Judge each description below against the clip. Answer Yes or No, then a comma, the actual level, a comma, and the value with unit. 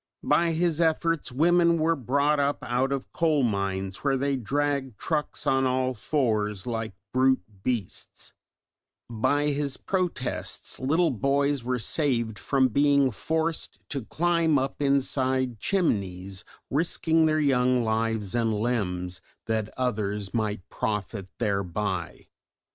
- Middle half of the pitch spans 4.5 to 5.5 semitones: Yes, average, 5.1 semitones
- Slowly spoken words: Yes, slow, 125 wpm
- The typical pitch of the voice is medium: No, low, 130 Hz